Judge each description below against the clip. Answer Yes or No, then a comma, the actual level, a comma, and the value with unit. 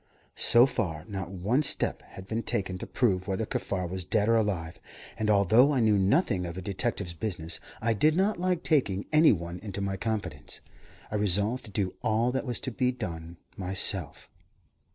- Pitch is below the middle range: Yes, low, 100 Hz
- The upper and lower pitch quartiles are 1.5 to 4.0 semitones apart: No, average, 4.4 semitones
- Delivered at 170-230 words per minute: Yes, average, 185 wpm